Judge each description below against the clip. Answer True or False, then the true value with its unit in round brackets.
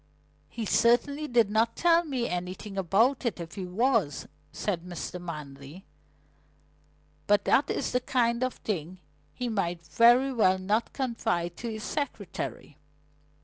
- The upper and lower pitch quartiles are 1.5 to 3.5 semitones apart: False (5.4 semitones)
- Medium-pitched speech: False (215 Hz)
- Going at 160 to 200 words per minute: False (140 wpm)